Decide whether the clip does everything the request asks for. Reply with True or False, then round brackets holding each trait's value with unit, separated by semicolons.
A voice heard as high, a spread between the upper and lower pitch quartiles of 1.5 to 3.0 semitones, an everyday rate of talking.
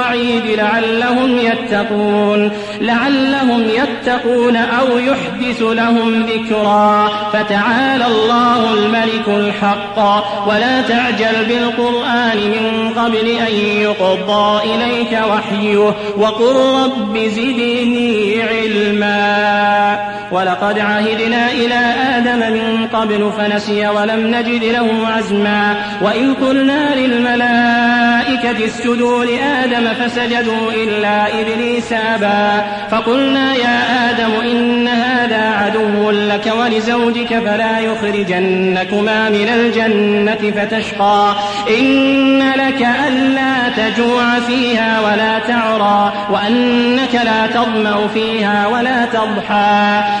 True (225 Hz; 2.4 semitones; 85 wpm)